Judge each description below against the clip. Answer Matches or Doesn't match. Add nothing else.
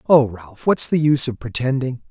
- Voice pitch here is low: Matches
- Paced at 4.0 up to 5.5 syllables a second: Matches